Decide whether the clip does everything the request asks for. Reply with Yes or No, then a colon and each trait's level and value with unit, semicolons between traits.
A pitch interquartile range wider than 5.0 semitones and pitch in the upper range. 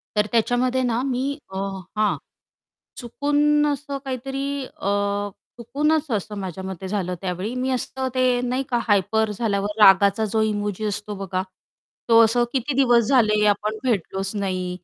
No: average, 4.1 semitones; high, 220 Hz